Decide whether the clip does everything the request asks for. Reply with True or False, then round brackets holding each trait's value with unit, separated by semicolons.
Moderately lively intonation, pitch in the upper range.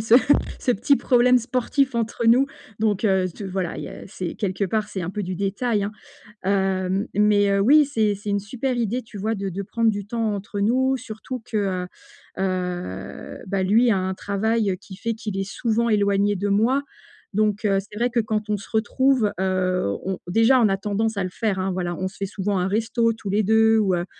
True (3.0 semitones; 205 Hz)